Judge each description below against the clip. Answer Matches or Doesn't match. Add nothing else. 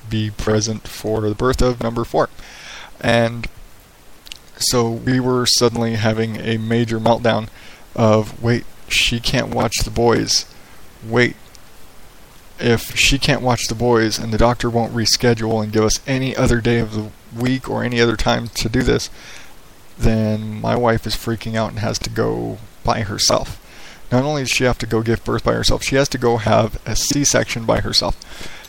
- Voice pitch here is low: Matches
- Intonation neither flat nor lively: Doesn't match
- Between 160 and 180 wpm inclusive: Matches